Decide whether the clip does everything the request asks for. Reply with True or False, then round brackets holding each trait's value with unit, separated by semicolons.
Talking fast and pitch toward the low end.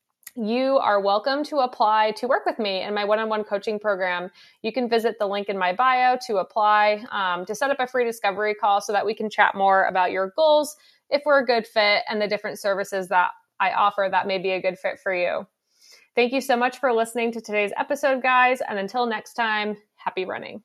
False (230 wpm; 215 Hz)